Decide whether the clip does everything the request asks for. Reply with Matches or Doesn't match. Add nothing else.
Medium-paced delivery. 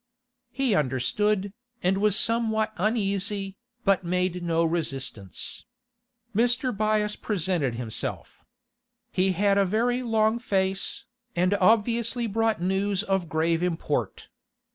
Doesn't match